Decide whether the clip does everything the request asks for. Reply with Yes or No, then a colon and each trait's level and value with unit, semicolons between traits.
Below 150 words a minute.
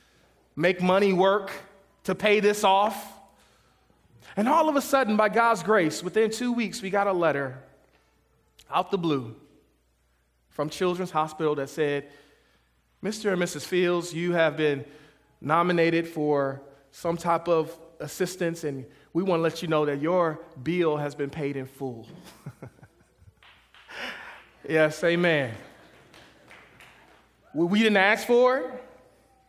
Yes: slow, 135 wpm